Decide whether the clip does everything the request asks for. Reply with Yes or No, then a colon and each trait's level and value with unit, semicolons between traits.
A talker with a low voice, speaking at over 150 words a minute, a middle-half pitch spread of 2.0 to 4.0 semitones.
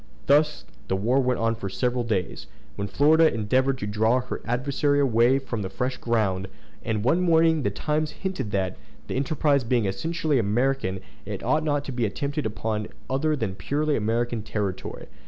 No: low, 125 Hz; average, 175 wpm; average, 5.2 semitones